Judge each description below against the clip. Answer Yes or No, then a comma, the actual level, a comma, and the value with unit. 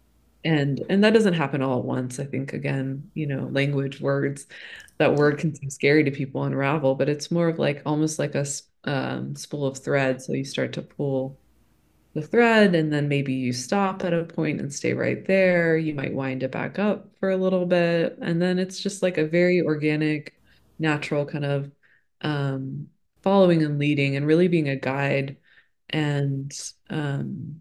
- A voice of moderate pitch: Yes, medium, 150 Hz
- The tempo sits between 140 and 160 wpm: No, average, 185 wpm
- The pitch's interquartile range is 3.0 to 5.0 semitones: Yes, average, 3.6 semitones